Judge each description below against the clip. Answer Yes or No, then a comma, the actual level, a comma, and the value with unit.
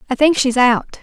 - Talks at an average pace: No, fast, 235 wpm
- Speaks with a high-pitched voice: Yes, very high, 265 Hz